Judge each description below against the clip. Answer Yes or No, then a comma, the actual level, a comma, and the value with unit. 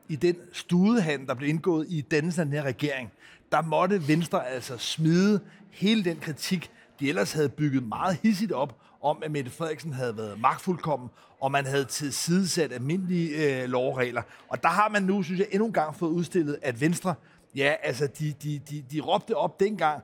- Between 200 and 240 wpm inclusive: No, average, 190 wpm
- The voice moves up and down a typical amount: Yes, average, 4.2 semitones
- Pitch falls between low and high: Yes, medium, 155 Hz